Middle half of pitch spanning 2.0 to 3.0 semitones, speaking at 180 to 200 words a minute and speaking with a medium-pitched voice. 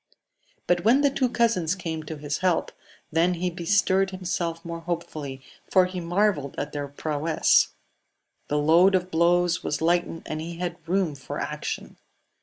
No: narrow, 2.6 semitones; average, 160 wpm; medium, 170 Hz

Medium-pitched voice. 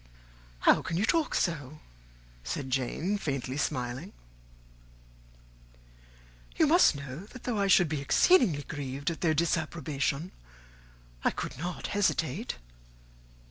Yes: medium, 160 Hz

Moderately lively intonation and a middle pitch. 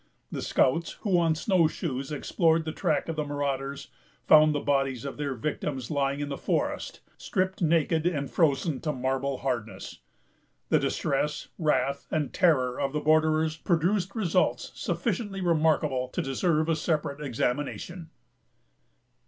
Yes: average, 3.2 semitones; medium, 150 Hz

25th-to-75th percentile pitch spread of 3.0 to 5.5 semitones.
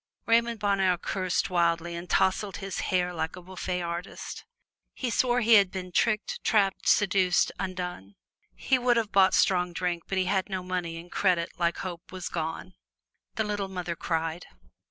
No: narrow, 2.4 semitones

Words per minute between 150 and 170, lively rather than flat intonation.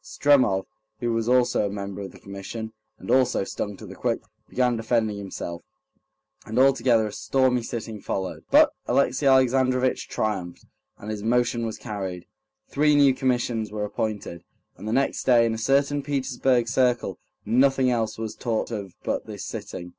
No: average, 165 wpm; average, 3.6 semitones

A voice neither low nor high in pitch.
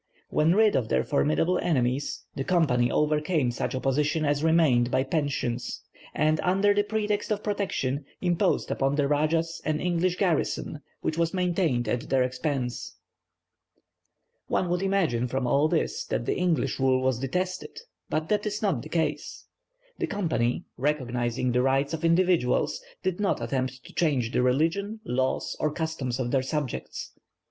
Yes: medium, 150 Hz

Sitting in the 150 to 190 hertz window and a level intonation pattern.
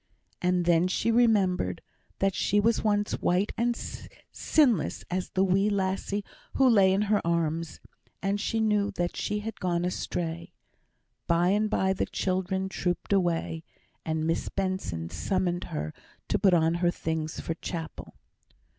No: medium, 185 Hz; average, 3.2 semitones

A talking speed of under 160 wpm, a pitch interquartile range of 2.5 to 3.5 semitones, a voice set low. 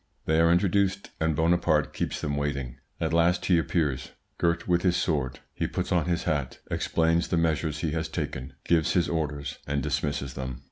No: average, 185 wpm; average, 2.9 semitones; very low, 80 Hz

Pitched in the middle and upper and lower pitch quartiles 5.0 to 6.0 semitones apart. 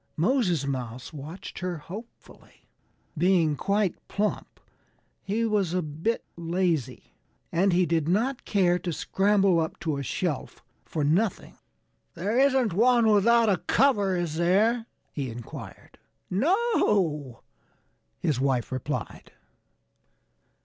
Yes: medium, 180 Hz; wide, 5.4 semitones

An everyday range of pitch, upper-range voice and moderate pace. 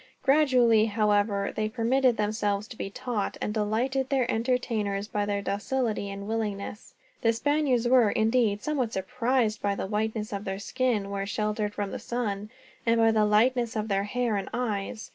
Yes: average, 3.1 semitones; high, 220 Hz; average, 170 wpm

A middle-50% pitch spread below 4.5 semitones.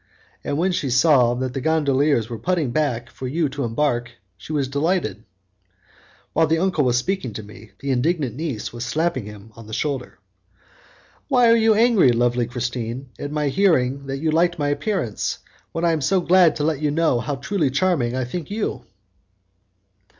No: average, 5.1 semitones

